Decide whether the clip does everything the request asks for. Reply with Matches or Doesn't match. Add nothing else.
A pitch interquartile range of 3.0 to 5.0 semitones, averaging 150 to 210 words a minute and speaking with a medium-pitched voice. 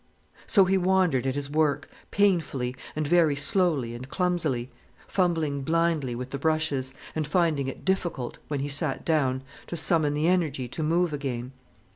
Matches